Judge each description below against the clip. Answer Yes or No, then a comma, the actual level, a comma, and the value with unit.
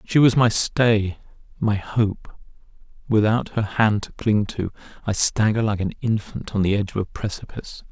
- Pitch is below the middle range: Yes, low, 105 Hz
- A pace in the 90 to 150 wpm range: No, average, 175 wpm